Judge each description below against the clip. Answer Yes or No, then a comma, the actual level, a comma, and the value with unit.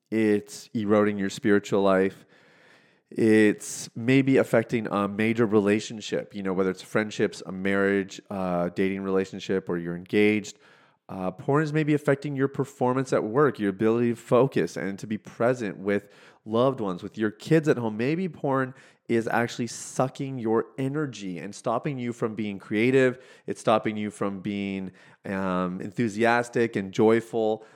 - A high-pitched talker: No, low, 110 Hz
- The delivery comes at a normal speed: Yes, average, 155 wpm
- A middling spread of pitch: Yes, average, 4.1 semitones